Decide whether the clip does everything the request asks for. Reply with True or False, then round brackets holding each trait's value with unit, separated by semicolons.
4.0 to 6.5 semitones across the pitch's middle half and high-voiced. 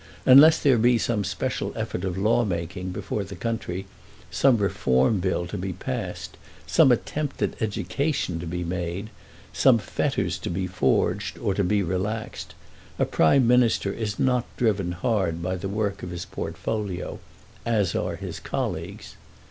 False (4.4 semitones; 100 Hz)